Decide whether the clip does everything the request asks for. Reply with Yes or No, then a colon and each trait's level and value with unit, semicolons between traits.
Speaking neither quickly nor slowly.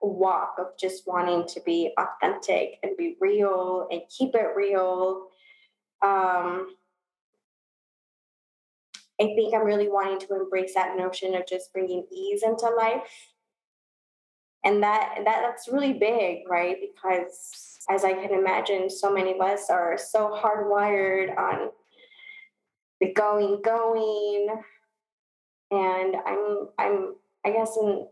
No: slow, 125 wpm